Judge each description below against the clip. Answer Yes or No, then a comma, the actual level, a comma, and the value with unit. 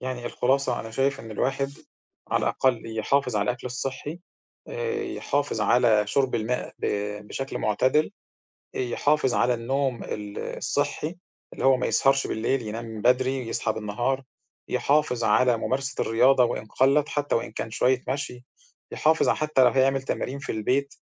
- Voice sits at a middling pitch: No, low, 130 Hz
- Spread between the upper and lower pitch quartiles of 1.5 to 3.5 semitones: Yes, average, 2.8 semitones